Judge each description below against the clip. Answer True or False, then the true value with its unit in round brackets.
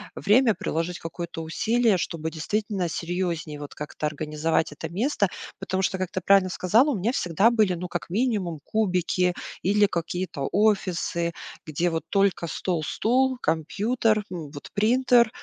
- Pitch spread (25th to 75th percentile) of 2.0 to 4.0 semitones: False (4.5 semitones)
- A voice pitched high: False (180 Hz)